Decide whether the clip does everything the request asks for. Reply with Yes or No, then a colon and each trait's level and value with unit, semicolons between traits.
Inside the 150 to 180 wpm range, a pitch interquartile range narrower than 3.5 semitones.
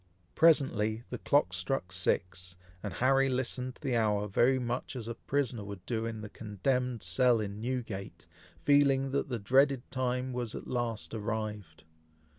No: average, 160 wpm; average, 3.8 semitones